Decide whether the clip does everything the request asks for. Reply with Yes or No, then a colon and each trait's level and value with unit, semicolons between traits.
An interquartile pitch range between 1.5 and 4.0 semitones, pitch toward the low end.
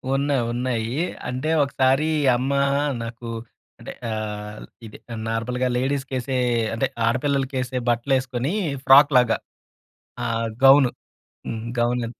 Yes: narrow, 2.6 semitones; low, 125 Hz